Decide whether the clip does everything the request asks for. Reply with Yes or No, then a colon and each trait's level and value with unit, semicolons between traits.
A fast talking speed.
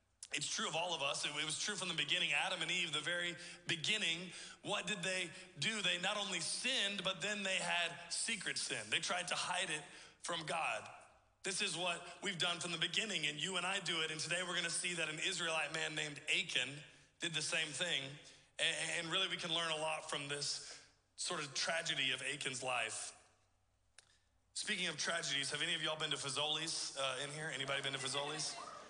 Yes: fast, 210 wpm